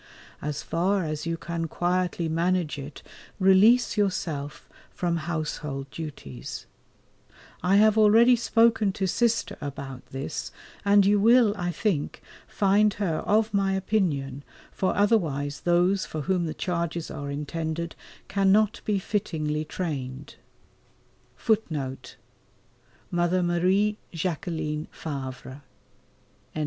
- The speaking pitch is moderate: Yes, medium, 175 Hz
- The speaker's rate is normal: No, slow, 100 wpm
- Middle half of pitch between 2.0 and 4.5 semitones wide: No, average, 5.0 semitones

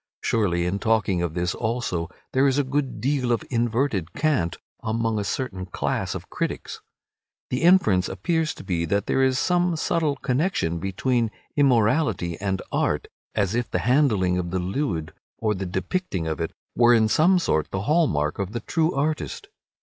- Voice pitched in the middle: No, low, 115 Hz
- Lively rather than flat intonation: Yes, wide, 7.2 semitones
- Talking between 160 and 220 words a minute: Yes, average, 175 wpm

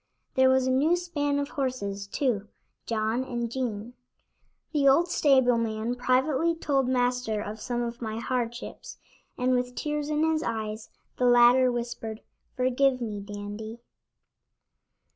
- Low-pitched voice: No, very high, 250 Hz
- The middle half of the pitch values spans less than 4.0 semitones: Yes, average, 3.1 semitones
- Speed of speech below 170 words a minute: Yes, average, 140 wpm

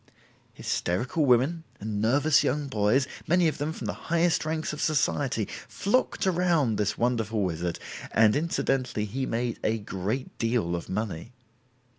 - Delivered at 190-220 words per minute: No, average, 145 wpm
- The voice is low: Yes, low, 125 Hz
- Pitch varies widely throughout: Yes, wide, 6.3 semitones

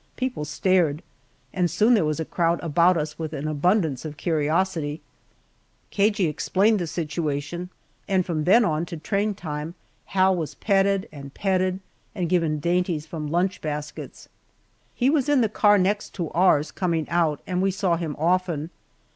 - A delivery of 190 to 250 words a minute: No, average, 165 wpm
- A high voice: No, medium, 175 Hz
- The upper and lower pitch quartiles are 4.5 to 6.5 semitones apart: No, average, 3.7 semitones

